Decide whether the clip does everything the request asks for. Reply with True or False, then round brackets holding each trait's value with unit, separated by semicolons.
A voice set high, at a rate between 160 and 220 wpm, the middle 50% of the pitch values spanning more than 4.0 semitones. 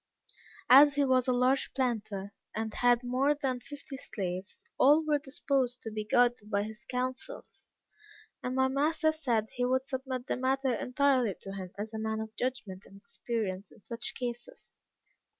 False (250 Hz; 170 wpm; 3.5 semitones)